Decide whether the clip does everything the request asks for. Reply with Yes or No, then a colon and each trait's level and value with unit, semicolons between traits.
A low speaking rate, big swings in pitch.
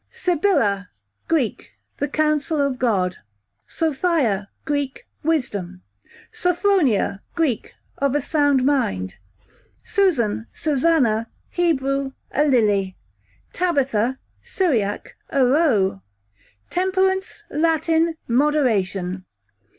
Yes: slow, 85 wpm; wide, 7.2 semitones